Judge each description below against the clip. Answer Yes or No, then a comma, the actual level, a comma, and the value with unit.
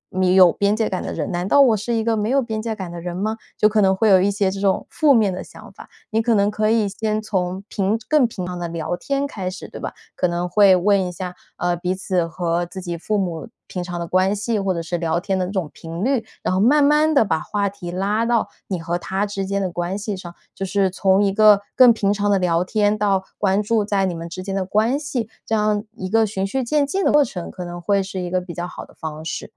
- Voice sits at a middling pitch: No, high, 195 Hz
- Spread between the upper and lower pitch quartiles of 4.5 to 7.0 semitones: No, average, 3.2 semitones